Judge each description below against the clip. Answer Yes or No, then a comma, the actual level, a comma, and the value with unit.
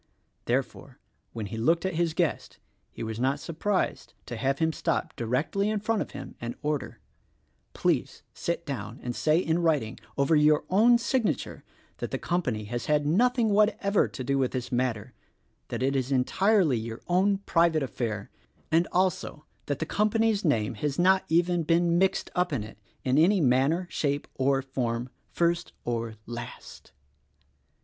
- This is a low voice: No, medium, 150 Hz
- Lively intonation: Yes, wide, 6.1 semitones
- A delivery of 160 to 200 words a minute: Yes, average, 170 wpm